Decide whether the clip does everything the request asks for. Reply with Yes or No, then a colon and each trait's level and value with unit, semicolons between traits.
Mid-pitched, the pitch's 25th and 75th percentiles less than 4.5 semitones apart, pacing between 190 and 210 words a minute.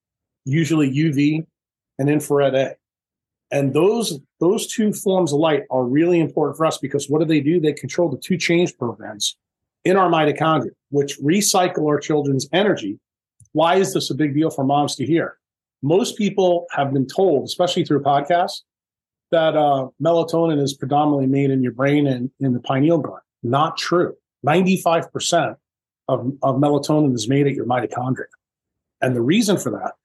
No: medium, 145 Hz; average, 3.5 semitones; average, 170 wpm